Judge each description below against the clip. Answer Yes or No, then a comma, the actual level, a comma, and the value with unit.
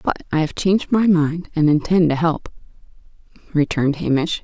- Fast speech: No, average, 160 wpm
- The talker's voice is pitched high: No, medium, 160 Hz